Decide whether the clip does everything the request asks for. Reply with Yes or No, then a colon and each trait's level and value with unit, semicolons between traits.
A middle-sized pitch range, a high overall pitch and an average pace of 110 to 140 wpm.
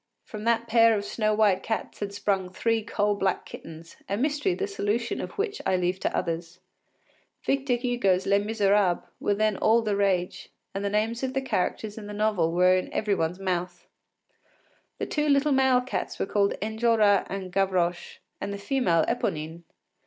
No: average, 3.8 semitones; high, 205 Hz; average, 180 wpm